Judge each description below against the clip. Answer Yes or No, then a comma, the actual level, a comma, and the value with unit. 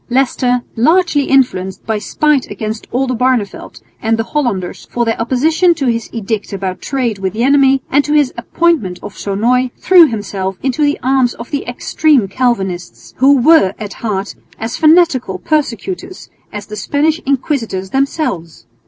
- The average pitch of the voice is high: Yes, high, 245 Hz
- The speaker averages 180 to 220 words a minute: No, average, 155 wpm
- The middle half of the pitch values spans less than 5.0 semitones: No, wide, 5.5 semitones